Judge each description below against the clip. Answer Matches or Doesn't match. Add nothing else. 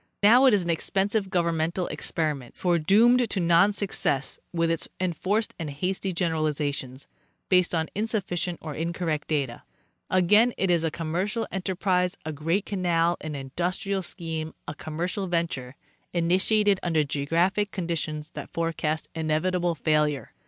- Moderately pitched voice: Matches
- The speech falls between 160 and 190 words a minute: Doesn't match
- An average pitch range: Matches